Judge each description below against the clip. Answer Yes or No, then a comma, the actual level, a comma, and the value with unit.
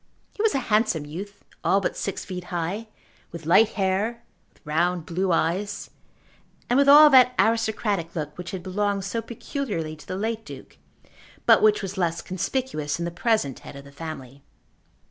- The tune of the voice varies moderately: Yes, average, 5.0 semitones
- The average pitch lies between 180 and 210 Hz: Yes, high, 190 Hz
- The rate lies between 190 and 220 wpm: No, average, 175 wpm